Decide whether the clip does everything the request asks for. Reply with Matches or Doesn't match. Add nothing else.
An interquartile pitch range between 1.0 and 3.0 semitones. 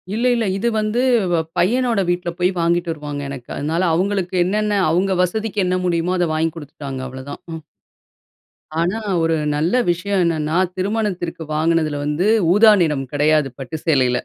Doesn't match